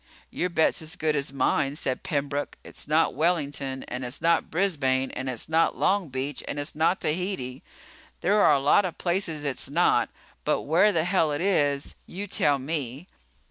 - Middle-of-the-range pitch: Yes, medium, 150 Hz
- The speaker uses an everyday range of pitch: Yes, average, 4.0 semitones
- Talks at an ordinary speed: Yes, average, 180 wpm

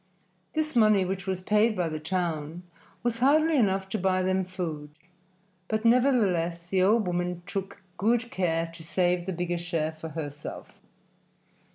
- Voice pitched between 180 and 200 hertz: Yes, medium, 185 Hz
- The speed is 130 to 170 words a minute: Yes, average, 155 wpm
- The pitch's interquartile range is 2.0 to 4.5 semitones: Yes, average, 4.0 semitones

